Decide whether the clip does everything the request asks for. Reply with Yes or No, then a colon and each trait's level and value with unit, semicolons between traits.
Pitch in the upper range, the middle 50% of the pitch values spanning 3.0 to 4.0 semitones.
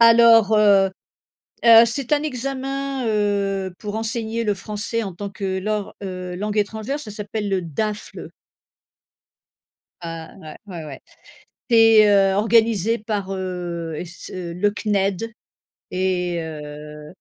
Yes: high, 205 Hz; average, 3.5 semitones